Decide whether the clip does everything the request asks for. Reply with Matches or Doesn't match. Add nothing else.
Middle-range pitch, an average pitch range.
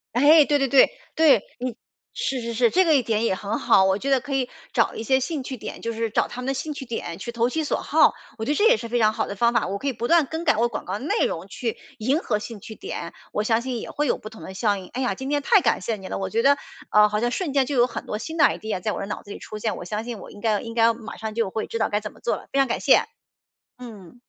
Doesn't match